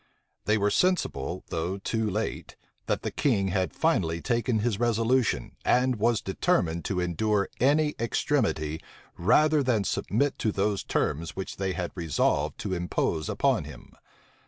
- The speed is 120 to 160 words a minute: Yes, average, 145 wpm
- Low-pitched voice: Yes, low, 100 Hz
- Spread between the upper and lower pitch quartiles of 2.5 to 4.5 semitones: No, average, 5.0 semitones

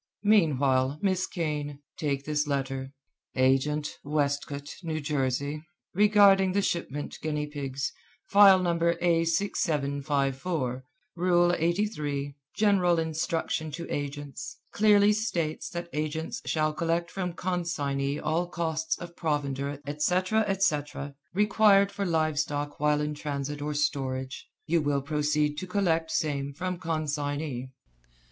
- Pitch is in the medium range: Yes, medium, 155 Hz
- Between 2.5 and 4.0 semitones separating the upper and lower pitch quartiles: Yes, average, 3.4 semitones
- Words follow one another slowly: Yes, slow, 115 wpm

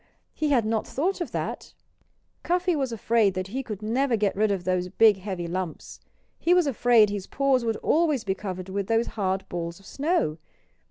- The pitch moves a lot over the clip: Yes, wide, 6.0 semitones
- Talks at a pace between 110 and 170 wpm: No, average, 195 wpm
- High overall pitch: Yes, high, 215 Hz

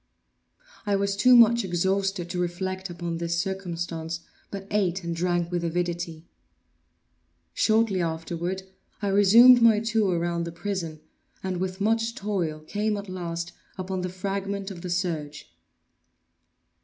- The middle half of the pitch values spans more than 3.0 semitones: No, average, 2.7 semitones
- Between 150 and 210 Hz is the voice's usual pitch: Yes, medium, 185 Hz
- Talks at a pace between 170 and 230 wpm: No, slow, 135 wpm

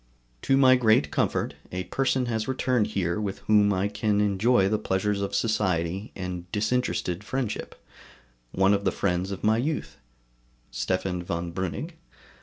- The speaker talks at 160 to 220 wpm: No, average, 150 wpm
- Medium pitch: No, low, 100 Hz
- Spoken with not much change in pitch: No, average, 3.3 semitones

